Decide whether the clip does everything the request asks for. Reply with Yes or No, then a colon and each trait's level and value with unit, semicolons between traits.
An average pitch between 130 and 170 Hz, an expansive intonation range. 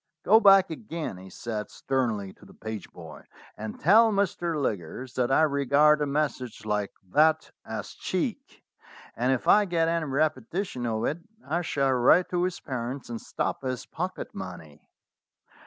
Yes: medium, 140 Hz; wide, 6.1 semitones